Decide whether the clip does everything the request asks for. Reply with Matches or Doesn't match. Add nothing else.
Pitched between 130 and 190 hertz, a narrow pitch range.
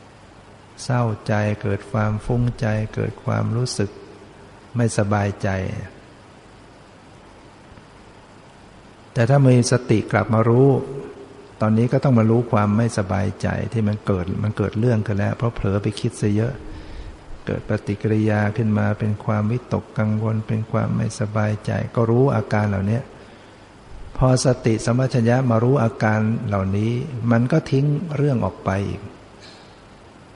Doesn't match